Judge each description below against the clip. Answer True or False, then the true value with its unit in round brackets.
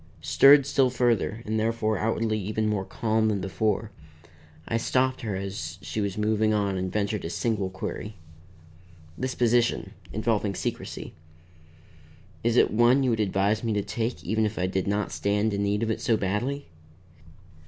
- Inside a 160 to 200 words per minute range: True (165 wpm)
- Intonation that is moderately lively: False (2.3 semitones)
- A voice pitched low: True (110 Hz)